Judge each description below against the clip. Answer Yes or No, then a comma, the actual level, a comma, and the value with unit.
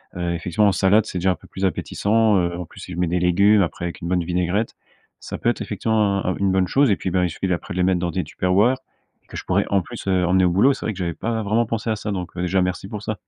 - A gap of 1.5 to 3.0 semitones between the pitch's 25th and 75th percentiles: Yes, average, 2.7 semitones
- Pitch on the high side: No, very low, 95 Hz